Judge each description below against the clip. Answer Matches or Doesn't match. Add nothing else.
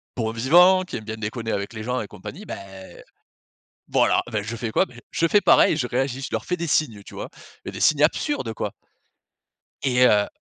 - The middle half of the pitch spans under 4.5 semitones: Doesn't match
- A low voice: Matches